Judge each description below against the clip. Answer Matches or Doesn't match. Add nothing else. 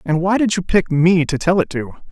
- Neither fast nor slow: Doesn't match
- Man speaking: Matches